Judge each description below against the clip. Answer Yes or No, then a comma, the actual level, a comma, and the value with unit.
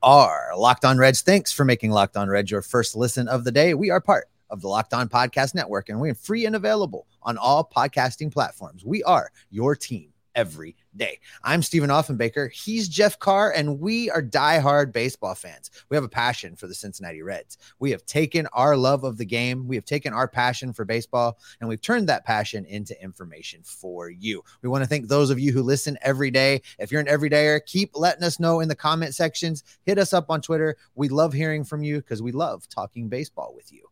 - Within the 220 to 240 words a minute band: Yes, fast, 225 wpm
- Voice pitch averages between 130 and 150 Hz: Yes, medium, 140 Hz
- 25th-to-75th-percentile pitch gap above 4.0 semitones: Yes, average, 4.8 semitones